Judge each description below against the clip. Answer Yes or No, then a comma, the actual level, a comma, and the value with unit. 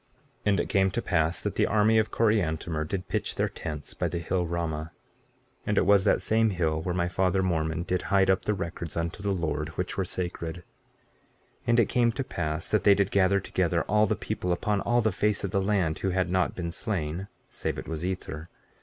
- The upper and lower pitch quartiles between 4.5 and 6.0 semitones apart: No, average, 3.1 semitones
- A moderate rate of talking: No, fast, 225 wpm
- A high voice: No, very low, 90 Hz